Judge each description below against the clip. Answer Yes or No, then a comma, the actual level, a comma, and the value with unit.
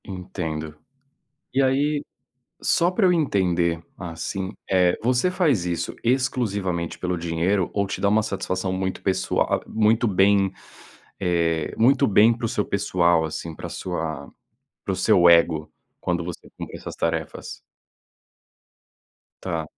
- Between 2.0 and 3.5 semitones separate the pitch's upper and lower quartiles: No, average, 4.4 semitones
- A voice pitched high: No, very low, 95 Hz